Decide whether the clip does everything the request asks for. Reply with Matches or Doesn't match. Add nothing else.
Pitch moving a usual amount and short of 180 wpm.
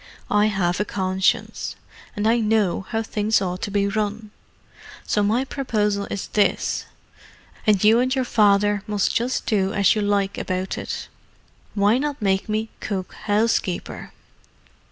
Doesn't match